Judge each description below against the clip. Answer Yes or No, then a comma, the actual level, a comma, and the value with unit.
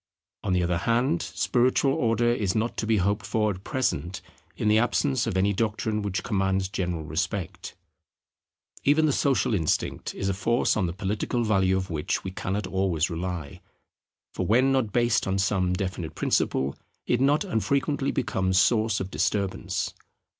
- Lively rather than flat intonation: No, average, 4.2 semitones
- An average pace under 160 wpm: No, average, 165 wpm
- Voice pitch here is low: Yes, low, 100 Hz